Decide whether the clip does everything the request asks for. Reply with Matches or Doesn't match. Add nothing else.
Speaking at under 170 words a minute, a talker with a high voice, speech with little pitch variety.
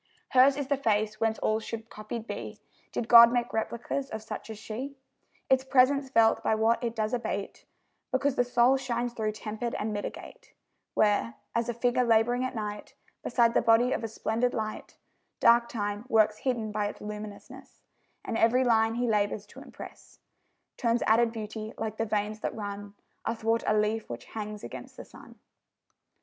Doesn't match